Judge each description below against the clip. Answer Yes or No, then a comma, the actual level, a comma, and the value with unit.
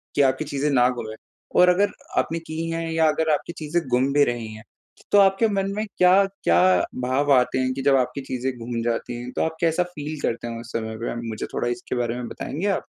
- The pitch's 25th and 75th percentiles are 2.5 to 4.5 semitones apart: No, average, 5.3 semitones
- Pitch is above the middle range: No, medium, 140 Hz